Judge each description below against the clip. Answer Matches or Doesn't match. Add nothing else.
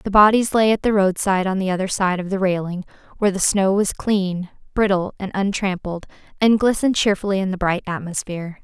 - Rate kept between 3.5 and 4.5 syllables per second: Doesn't match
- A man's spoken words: Doesn't match